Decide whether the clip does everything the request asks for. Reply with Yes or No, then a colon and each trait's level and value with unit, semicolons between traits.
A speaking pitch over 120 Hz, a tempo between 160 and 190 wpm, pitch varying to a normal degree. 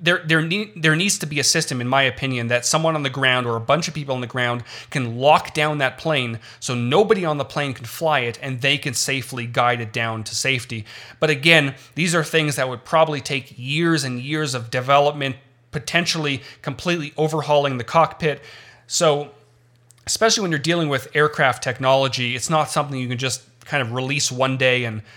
No: medium, 140 Hz; fast, 205 wpm; average, 3.8 semitones